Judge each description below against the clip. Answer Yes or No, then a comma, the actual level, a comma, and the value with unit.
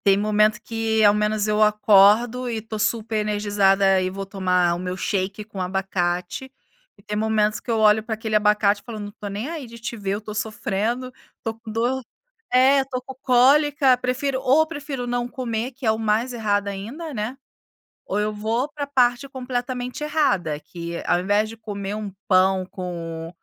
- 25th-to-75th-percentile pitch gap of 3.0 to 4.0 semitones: Yes, average, 3.6 semitones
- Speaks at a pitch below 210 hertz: No, high, 215 Hz